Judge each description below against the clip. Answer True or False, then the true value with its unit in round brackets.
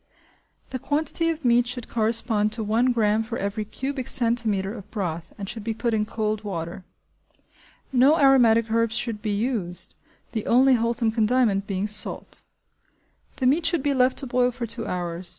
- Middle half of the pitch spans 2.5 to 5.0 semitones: True (3.1 semitones)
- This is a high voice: True (230 Hz)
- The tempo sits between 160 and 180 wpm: True (170 wpm)